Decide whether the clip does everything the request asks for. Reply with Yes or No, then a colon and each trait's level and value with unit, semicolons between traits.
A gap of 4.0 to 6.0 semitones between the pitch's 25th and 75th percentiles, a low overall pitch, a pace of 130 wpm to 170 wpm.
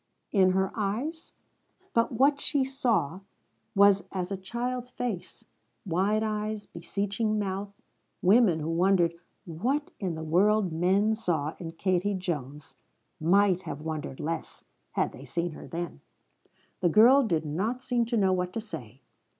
No: average, 4.5 semitones; high, 190 Hz; average, 145 wpm